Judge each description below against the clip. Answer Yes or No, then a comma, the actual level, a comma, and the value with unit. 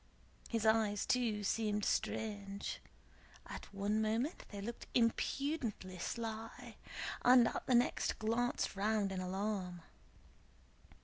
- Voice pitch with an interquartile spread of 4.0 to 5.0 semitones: No, narrow, 2.6 semitones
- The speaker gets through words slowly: Yes, slow, 110 wpm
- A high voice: Yes, high, 220 Hz